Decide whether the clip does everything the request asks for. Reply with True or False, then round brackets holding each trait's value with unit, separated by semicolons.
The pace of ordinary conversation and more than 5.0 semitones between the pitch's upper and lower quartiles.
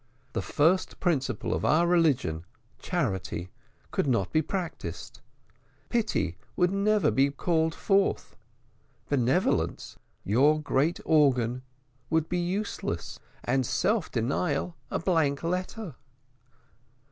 False (105 wpm; 5.4 semitones)